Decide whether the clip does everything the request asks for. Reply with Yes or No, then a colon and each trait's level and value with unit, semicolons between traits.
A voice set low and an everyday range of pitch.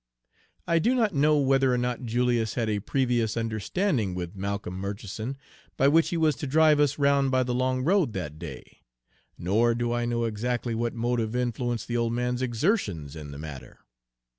Yes: low, 120 Hz; average, 3.9 semitones